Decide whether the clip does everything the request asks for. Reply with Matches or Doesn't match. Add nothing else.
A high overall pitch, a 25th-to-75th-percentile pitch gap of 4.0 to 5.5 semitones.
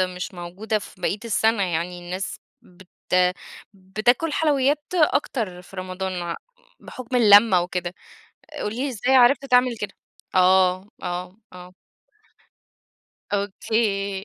Matches